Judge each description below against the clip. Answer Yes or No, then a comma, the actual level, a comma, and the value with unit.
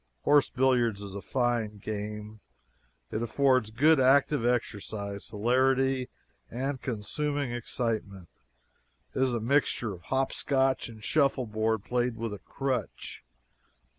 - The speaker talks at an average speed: No, slow, 120 wpm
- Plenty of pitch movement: No, average, 3.7 semitones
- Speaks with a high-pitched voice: No, low, 120 Hz